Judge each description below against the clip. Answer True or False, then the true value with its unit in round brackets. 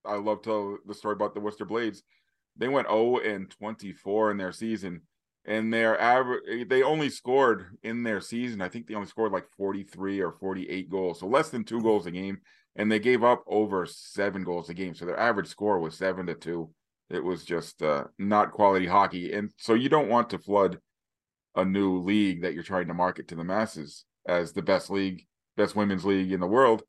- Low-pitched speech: True (100 Hz)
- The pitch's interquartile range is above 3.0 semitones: False (2.6 semitones)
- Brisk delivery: True (215 wpm)